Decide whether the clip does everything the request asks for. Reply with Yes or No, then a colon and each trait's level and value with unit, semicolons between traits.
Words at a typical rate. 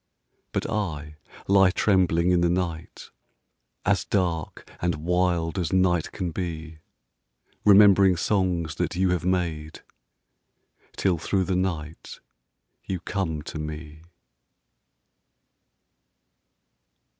No: slow, 100 wpm